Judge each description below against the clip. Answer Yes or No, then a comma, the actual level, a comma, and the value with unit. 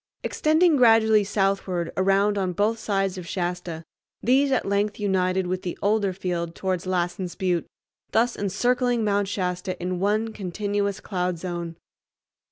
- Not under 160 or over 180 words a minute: No, average, 140 wpm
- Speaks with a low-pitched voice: No, high, 195 Hz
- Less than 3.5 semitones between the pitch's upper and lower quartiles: Yes, average, 2.8 semitones